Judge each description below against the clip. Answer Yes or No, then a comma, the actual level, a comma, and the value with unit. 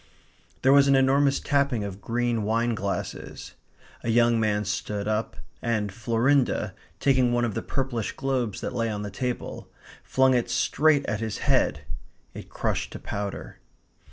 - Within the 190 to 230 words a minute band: No, average, 155 wpm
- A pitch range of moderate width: Yes, average, 3.9 semitones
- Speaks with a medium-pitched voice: No, low, 120 Hz